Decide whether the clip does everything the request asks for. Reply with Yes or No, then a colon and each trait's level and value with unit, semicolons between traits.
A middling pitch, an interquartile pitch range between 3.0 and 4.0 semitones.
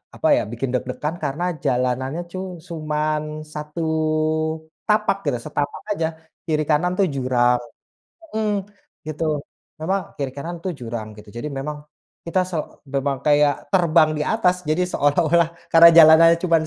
Yes: medium, 155 Hz; average, 3.5 semitones